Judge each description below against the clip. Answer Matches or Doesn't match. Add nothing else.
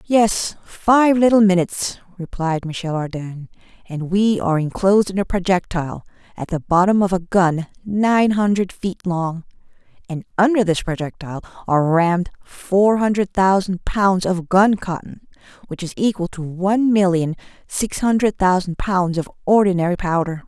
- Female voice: Matches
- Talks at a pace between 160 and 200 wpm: Doesn't match